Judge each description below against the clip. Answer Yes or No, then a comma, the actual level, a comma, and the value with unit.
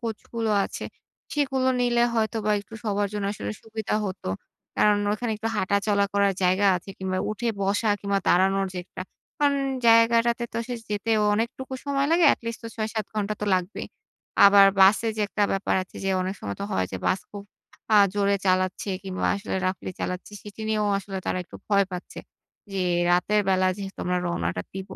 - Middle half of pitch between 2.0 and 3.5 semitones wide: Yes, average, 2.9 semitones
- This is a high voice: Yes, high, 205 Hz